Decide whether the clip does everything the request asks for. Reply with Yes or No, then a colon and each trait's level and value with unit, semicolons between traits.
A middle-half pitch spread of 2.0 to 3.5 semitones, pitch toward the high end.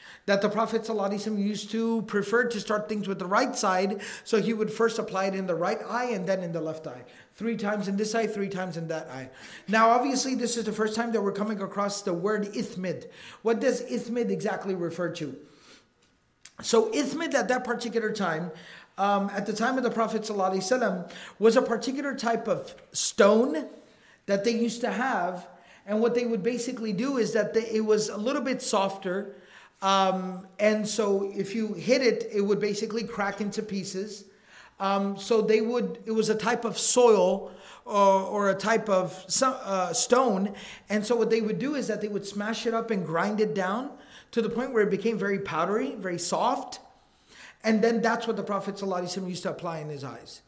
Yes: average, 3.0 semitones; high, 215 Hz